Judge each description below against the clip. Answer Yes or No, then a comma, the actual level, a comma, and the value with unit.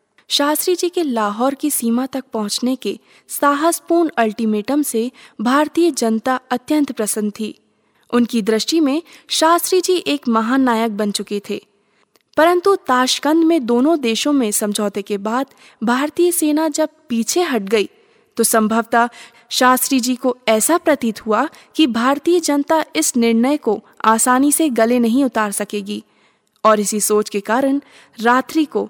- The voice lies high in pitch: Yes, very high, 250 Hz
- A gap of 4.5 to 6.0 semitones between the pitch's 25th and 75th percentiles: Yes, wide, 5.4 semitones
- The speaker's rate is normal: Yes, average, 145 wpm